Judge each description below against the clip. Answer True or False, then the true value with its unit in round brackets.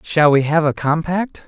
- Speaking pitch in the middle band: True (160 Hz)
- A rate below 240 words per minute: True (205 wpm)